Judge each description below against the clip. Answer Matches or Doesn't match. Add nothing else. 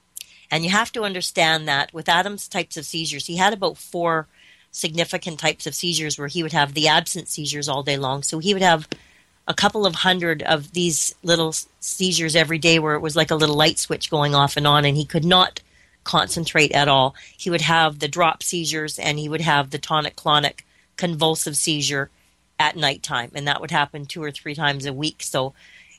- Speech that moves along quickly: Matches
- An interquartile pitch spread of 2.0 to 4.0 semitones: Matches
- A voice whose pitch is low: Doesn't match